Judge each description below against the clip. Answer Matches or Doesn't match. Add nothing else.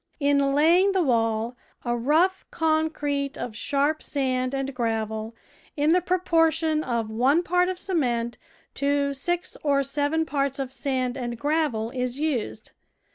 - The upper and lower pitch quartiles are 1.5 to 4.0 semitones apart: Doesn't match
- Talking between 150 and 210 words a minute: Doesn't match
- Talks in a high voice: Matches